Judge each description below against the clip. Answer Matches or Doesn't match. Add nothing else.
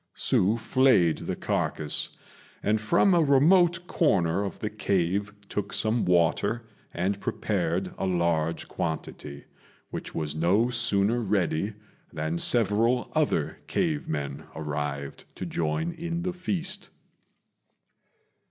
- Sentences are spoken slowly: Matches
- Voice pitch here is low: Matches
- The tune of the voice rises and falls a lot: Matches